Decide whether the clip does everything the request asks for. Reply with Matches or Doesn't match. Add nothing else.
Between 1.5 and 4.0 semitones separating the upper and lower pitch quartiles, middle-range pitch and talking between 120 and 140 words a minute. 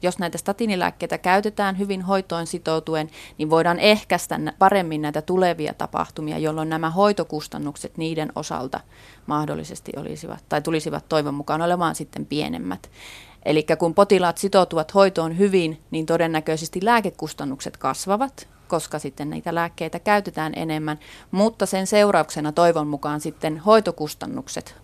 Matches